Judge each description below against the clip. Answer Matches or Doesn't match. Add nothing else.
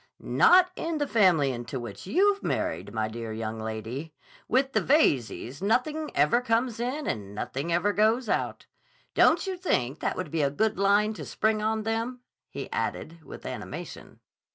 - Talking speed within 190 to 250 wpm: Doesn't match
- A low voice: Doesn't match